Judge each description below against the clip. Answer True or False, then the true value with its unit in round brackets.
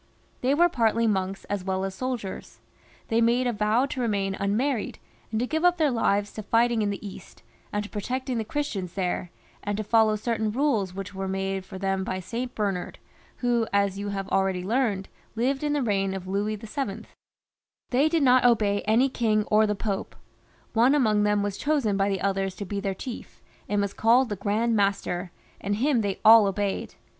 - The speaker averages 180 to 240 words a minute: True (200 wpm)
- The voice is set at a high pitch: True (210 Hz)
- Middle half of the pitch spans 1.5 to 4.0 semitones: True (3.5 semitones)